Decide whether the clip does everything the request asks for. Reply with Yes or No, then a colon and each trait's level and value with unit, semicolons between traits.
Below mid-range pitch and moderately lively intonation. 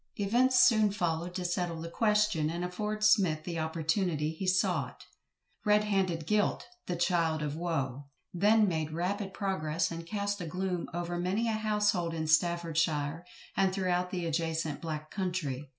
No: medium, 175 Hz; average, 3.7 semitones